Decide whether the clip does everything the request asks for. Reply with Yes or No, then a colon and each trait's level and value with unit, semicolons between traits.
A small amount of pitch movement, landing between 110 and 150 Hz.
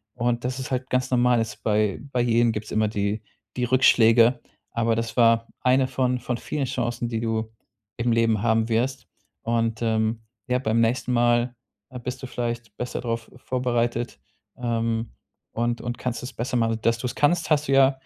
Yes: narrow, 1.7 semitones; low, 120 Hz